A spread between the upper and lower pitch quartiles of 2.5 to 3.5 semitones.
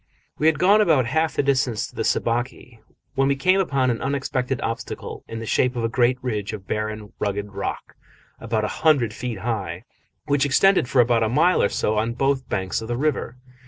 No: average, 4.0 semitones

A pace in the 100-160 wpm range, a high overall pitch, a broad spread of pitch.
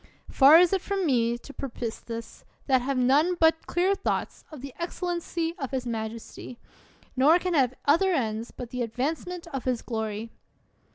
No: average, 170 wpm; very high, 270 Hz; wide, 5.9 semitones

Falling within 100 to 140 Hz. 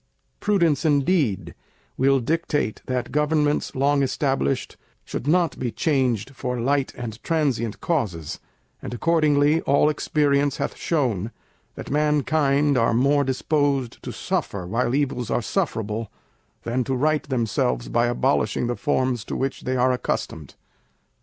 Yes: low, 135 Hz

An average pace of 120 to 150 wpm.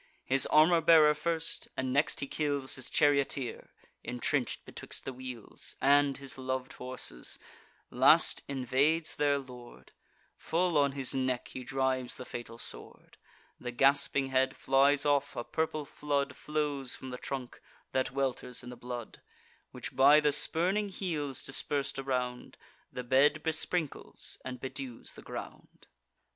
Yes: average, 140 wpm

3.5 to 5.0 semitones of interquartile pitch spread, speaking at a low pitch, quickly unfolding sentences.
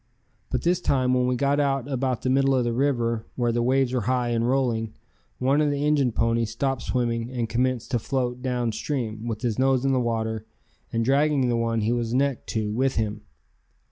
No: narrow, 2.5 semitones; low, 125 Hz; fast, 210 wpm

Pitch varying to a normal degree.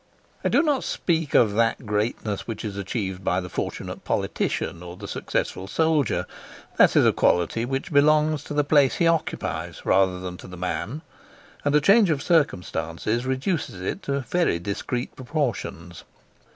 No: wide, 8.1 semitones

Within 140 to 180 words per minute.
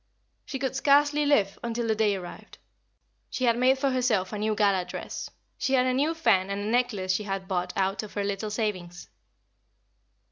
No: average, 190 wpm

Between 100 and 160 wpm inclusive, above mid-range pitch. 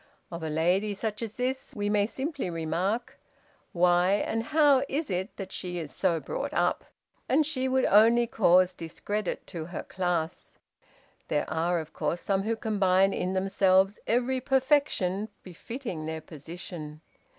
Yes: average, 150 wpm; high, 195 Hz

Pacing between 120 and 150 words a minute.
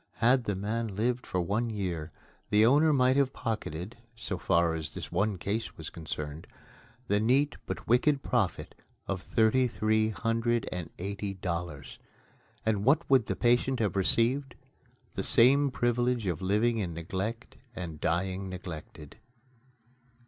Yes: average, 145 wpm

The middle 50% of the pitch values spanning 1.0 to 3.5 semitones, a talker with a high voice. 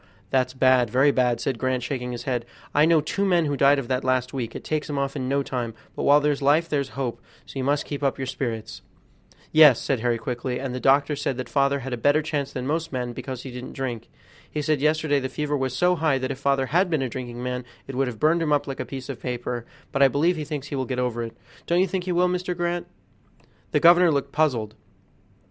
No: average, 3.0 semitones; low, 135 Hz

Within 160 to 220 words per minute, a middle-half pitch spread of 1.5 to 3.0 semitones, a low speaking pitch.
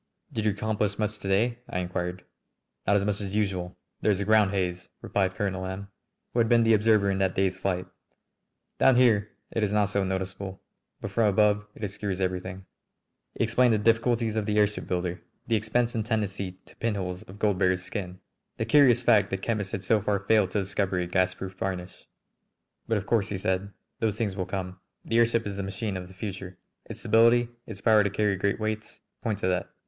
Yes: fast, 205 wpm; narrow, 2.5 semitones; low, 100 Hz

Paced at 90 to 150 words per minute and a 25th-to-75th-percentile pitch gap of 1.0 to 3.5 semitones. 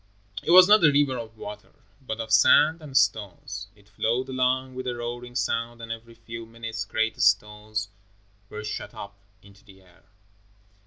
No: average, 170 wpm; average, 3.2 semitones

